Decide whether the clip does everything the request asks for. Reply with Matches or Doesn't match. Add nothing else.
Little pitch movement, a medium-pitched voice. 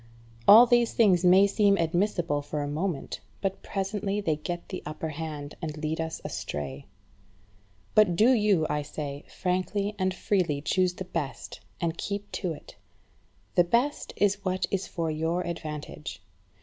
Doesn't match